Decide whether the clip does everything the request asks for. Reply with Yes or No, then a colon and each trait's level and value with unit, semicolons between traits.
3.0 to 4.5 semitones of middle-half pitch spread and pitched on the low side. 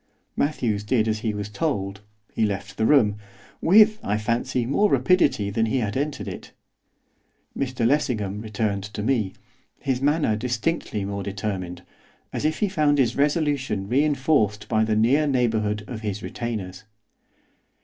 No: average, 5.2 semitones; low, 115 Hz